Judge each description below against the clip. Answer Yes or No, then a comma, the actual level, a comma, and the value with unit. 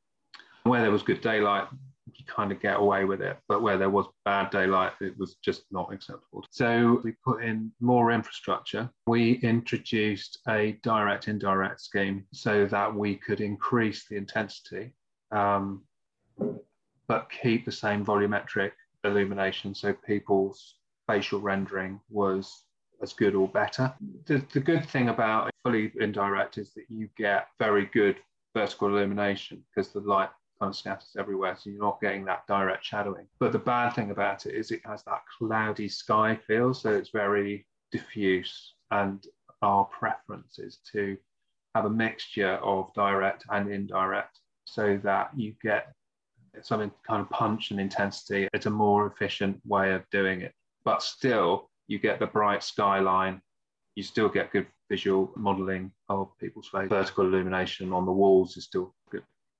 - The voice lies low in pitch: Yes, low, 100 Hz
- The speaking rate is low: No, average, 155 wpm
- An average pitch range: No, narrow, 2.1 semitones